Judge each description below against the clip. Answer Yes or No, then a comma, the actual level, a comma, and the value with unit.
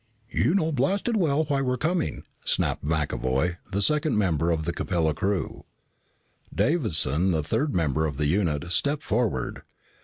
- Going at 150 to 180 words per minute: Yes, average, 155 wpm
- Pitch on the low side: Yes, very low, 95 Hz